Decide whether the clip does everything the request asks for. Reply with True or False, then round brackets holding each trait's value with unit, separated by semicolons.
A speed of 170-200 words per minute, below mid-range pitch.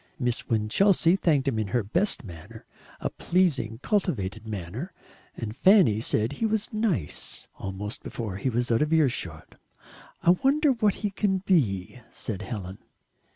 False (150 wpm; 125 Hz)